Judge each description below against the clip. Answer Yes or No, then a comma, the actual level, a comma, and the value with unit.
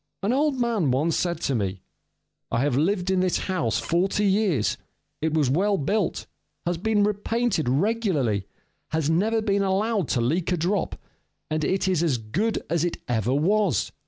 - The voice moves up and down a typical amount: No, wide, 6.1 semitones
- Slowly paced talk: No, average, 170 wpm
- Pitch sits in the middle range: Yes, medium, 175 Hz